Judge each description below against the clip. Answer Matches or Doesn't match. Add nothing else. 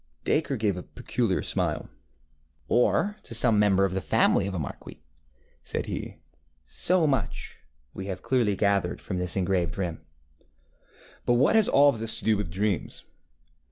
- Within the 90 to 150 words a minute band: Doesn't match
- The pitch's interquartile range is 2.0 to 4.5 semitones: Doesn't match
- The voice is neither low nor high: Doesn't match